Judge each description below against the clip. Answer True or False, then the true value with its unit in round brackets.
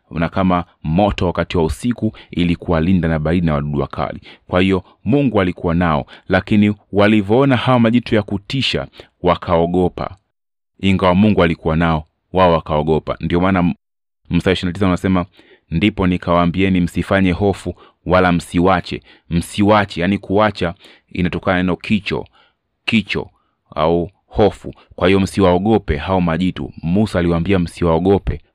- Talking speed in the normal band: True (120 wpm)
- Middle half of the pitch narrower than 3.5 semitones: True (2.8 semitones)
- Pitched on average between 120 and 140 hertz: False (90 Hz)